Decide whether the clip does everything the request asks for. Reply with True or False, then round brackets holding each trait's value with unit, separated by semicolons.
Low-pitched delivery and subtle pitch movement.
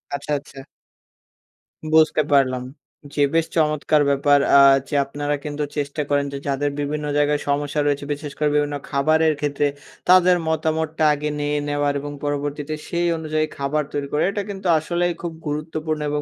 False (150 Hz; 1.5 semitones)